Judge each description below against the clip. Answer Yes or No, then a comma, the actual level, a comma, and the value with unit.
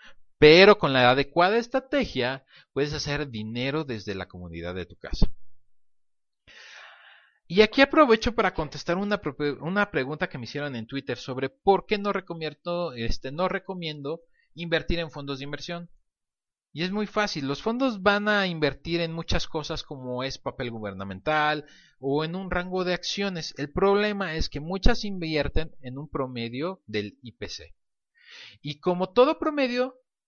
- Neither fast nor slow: Yes, average, 155 wpm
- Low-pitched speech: No, medium, 155 Hz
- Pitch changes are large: Yes, wide, 6.2 semitones